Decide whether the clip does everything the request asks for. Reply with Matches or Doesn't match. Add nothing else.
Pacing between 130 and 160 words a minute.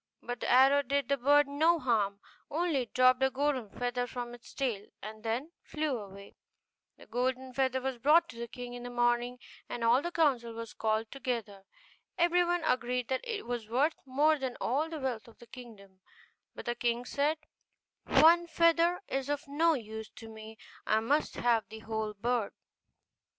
Doesn't match